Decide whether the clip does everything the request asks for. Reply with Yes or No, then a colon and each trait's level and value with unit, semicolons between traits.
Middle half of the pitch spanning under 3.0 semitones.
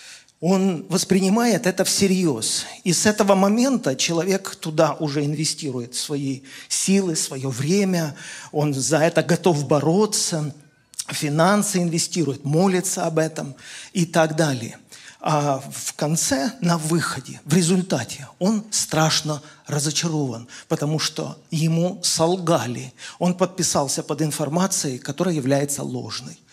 No: average, 3.7 semitones